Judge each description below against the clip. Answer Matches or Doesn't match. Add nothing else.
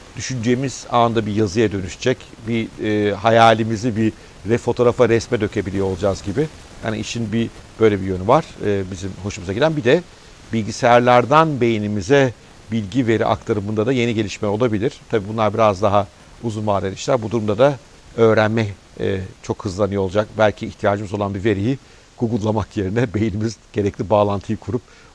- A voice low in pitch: Matches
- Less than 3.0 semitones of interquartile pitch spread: Matches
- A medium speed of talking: Doesn't match